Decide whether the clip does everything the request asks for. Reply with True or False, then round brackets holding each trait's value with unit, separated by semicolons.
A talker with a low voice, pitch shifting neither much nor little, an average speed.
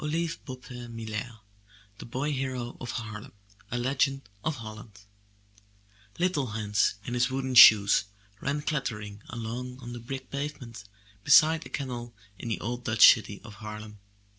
True (120 Hz; 3.4 semitones; 150 wpm)